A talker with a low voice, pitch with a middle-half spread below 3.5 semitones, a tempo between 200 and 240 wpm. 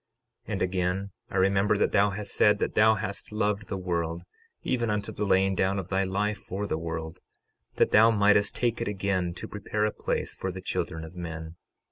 Yes: low, 100 Hz; narrow, 2.4 semitones; fast, 205 wpm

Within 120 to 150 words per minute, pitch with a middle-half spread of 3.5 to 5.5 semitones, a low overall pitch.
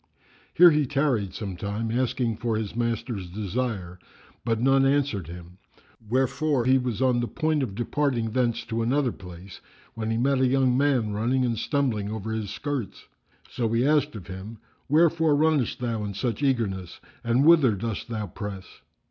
No: average, 170 wpm; average, 4.3 semitones; low, 120 Hz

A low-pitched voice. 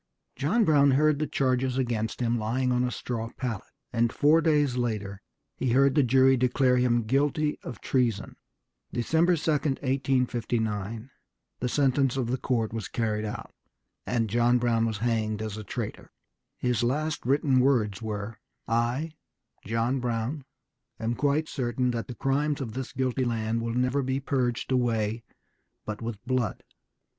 Yes: low, 125 Hz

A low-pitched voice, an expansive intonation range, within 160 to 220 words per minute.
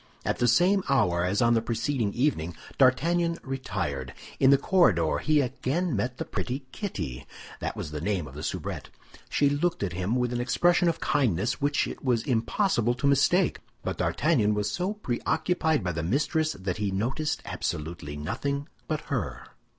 Yes: low, 125 Hz; wide, 7.4 semitones; average, 175 wpm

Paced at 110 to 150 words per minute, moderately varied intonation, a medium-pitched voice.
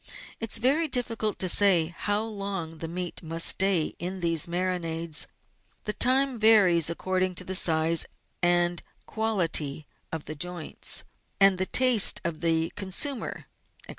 Yes: average, 145 wpm; average, 4.2 semitones; medium, 180 Hz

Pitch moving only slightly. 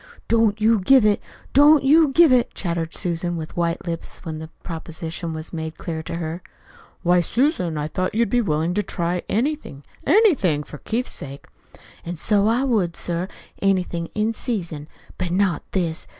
No: wide, 5.5 semitones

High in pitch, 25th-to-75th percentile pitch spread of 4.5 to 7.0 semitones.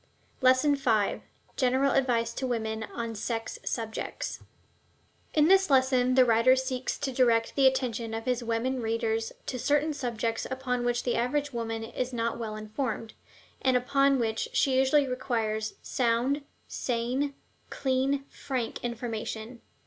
No: high, 245 Hz; narrow, 2.5 semitones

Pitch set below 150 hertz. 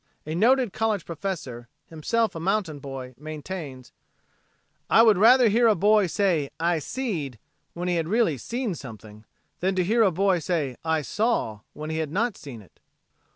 No: medium, 175 Hz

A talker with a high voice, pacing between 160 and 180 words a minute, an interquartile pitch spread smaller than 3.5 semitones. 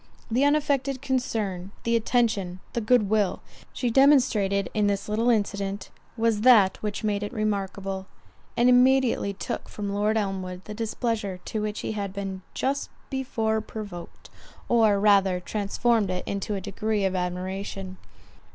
No: high, 210 Hz; average, 145 wpm; average, 3.0 semitones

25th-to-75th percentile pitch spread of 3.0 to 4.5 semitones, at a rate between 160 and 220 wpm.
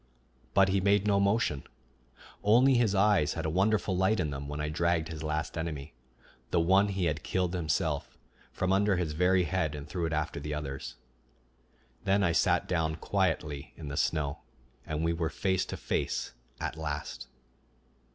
Yes: average, 3.9 semitones; average, 175 wpm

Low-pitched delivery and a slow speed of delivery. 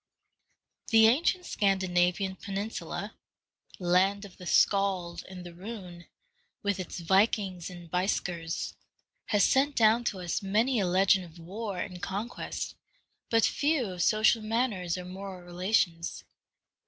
No: high, 195 Hz; slow, 130 wpm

